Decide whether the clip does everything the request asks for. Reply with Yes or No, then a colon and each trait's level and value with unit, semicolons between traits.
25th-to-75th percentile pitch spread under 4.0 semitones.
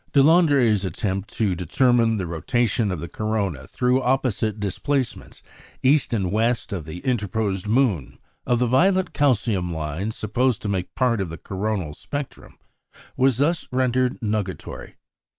No: average, 5.1 semitones